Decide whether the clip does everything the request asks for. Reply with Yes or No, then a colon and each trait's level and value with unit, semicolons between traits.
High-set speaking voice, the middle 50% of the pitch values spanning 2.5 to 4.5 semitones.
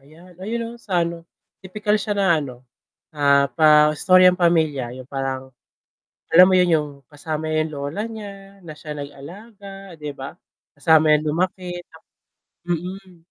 No: medium, 165 Hz; average, 4.1 semitones